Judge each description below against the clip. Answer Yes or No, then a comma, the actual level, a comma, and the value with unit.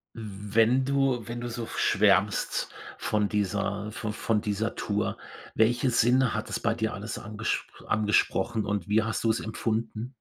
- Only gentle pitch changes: Yes, narrow, 1.9 semitones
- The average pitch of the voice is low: Yes, low, 110 Hz